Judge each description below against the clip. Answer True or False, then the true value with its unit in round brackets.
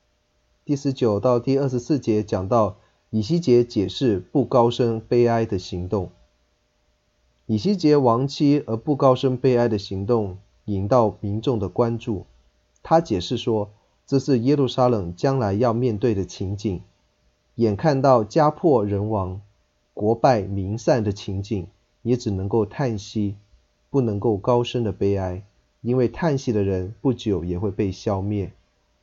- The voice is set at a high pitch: False (110 Hz)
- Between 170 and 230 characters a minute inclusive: True (215 characters per minute)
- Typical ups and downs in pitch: True (4.5 semitones)